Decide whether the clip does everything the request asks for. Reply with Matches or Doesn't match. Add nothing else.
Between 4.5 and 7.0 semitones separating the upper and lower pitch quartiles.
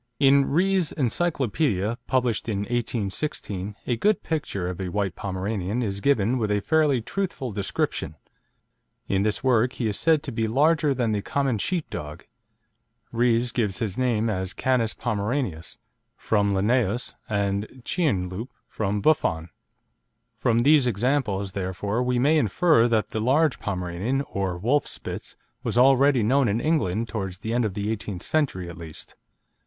Matches